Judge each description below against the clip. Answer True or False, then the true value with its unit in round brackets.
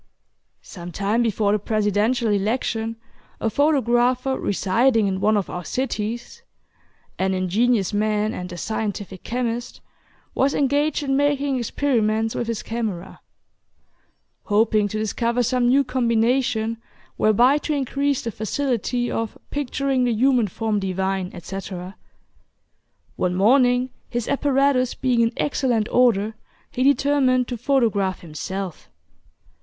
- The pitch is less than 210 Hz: False (230 Hz)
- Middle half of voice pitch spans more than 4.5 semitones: False (3.8 semitones)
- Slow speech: True (120 wpm)